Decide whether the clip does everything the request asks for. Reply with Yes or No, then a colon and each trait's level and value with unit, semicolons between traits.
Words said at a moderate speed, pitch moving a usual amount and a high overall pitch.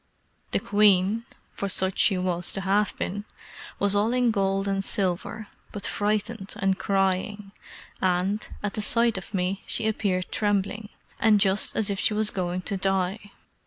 No: average, 160 wpm; narrow, 1.8 semitones; high, 200 Hz